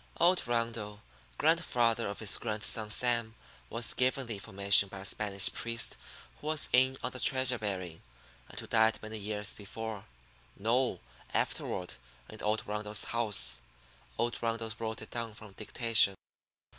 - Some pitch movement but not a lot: No, narrow, 2.3 semitones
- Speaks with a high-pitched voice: No, low, 110 Hz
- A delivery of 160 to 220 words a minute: No, average, 145 wpm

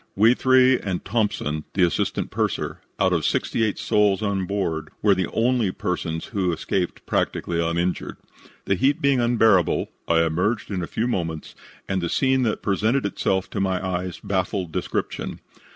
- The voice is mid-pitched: No, very low, 95 Hz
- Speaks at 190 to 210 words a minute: No, average, 165 wpm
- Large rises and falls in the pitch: No, average, 4.1 semitones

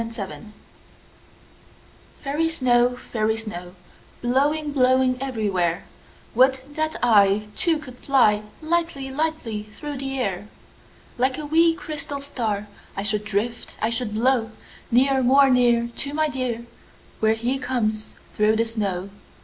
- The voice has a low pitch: No, high, 245 Hz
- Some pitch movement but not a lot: Yes, average, 4.2 semitones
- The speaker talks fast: No, slow, 135 wpm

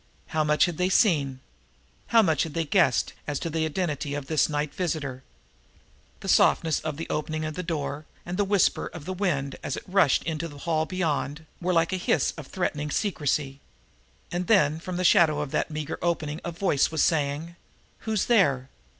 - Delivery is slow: No, average, 195 wpm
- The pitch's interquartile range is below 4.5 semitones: Yes, average, 3.3 semitones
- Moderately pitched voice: Yes, medium, 160 Hz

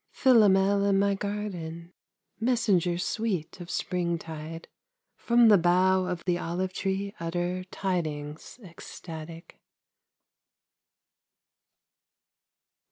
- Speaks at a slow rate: Yes, slow, 85 wpm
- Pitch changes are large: No, average, 2.9 semitones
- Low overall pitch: No, medium, 180 Hz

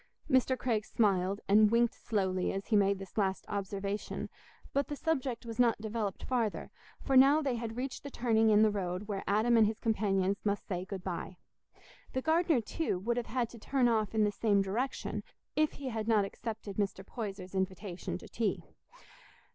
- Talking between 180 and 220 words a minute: Yes, average, 185 wpm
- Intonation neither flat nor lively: Yes, average, 3.5 semitones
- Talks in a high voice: Yes, high, 215 Hz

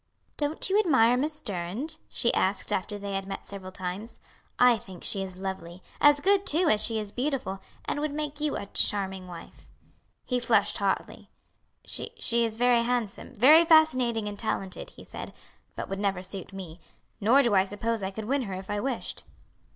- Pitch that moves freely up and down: Yes, wide, 5.8 semitones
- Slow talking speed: No, average, 185 wpm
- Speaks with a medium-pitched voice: No, high, 220 Hz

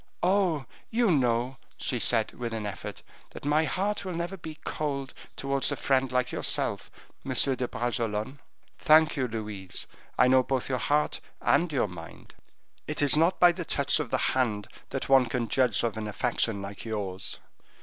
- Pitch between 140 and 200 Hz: No, low, 130 Hz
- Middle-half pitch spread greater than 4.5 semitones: Yes, average, 4.9 semitones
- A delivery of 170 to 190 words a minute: Yes, average, 175 wpm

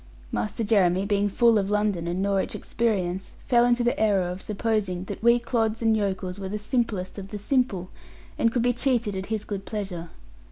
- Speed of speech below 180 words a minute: No, average, 195 wpm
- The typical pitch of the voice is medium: No, high, 205 Hz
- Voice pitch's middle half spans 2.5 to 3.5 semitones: Yes, average, 3.2 semitones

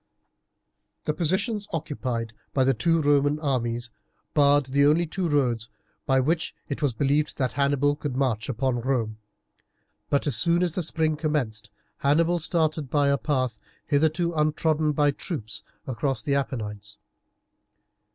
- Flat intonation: No, average, 3.3 semitones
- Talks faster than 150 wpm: No, average, 140 wpm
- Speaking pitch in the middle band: Yes, medium, 145 Hz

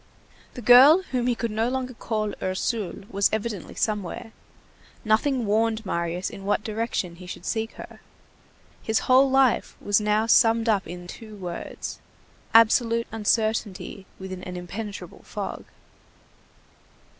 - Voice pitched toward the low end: No, high, 220 Hz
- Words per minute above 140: No, slow, 135 wpm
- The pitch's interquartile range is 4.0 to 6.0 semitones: No, average, 3.0 semitones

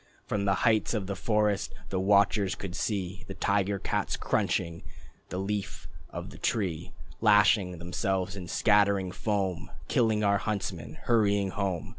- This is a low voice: Yes, low, 100 Hz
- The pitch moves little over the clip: Yes, narrow, 1.8 semitones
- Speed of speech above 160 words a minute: No, average, 145 wpm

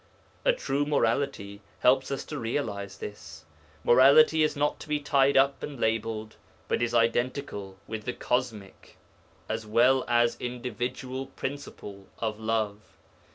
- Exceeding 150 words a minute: No, slow, 135 wpm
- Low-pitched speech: Yes, low, 120 Hz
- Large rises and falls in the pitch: No, average, 4.0 semitones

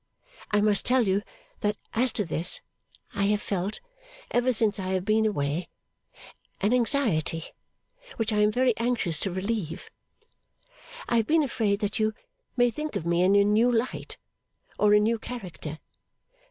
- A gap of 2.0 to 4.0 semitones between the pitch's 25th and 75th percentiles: Yes, average, 3.6 semitones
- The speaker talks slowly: No, average, 160 wpm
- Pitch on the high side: Yes, high, 210 Hz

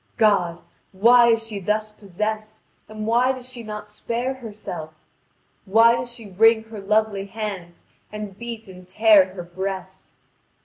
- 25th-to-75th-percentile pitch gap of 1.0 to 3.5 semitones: Yes, average, 2.8 semitones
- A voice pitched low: No, high, 215 Hz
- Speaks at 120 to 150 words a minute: Yes, average, 145 wpm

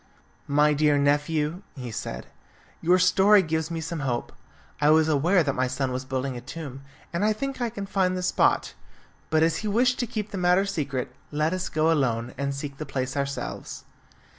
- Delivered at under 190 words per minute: No, average, 195 wpm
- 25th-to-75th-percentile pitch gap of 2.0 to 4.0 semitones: No, average, 4.9 semitones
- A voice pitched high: No, medium, 155 Hz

